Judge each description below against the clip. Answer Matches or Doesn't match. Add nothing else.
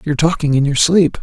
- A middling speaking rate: Doesn't match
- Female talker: Doesn't match